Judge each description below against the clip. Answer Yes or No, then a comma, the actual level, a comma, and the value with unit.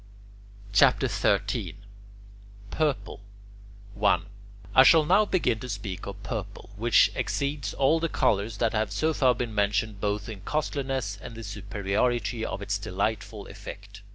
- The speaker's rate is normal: Yes, average, 145 wpm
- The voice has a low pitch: Yes, low, 110 Hz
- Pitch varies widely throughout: No, average, 4.7 semitones